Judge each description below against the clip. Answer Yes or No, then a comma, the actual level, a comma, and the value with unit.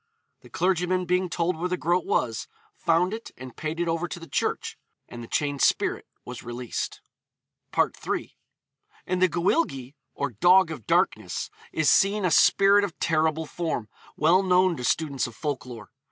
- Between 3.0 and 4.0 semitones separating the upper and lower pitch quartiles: No, average, 5.0 semitones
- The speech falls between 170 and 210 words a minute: Yes, average, 180 wpm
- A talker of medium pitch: Yes, medium, 165 Hz